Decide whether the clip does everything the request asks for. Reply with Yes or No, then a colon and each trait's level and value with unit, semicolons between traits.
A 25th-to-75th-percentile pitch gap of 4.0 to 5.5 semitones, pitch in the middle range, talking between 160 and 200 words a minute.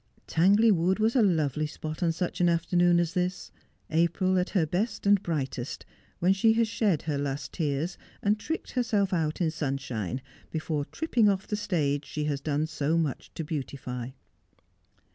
Yes: average, 4.6 semitones; medium, 170 Hz; average, 175 wpm